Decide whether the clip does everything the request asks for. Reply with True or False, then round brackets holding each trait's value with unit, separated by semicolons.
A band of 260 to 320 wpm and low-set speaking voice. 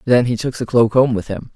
True (310 wpm; 120 Hz)